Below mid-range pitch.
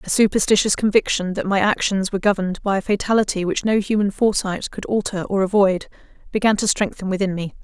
No: high, 200 Hz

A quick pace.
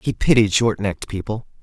No: average, 185 wpm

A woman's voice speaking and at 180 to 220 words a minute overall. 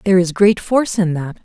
No: female; fast, 250 wpm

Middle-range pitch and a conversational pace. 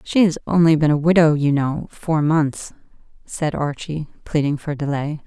Yes: medium, 155 Hz; average, 170 wpm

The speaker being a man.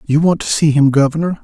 Yes: male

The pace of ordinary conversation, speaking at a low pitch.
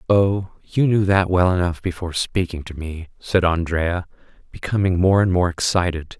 Yes: average, 165 wpm; very low, 90 Hz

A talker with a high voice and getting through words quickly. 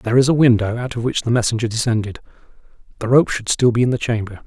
No: low, 115 Hz; fast, 240 wpm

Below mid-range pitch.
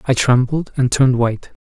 Yes: low, 125 Hz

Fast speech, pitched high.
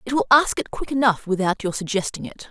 Yes: fast, 240 wpm; high, 220 Hz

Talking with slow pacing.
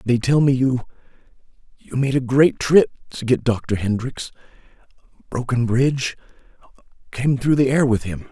Yes: slow, 130 wpm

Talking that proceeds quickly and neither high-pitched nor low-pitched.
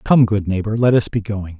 No: fast, 265 wpm; low, 105 Hz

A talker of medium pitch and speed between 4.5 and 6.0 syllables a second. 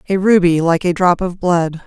Yes: medium, 175 Hz; 4.8 syllables/s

